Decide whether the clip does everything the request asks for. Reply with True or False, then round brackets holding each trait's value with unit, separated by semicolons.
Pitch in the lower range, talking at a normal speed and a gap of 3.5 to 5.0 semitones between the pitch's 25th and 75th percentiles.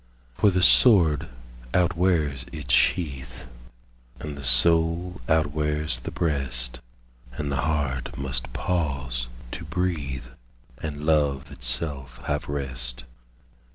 False (75 Hz; 105 wpm; 3.9 semitones)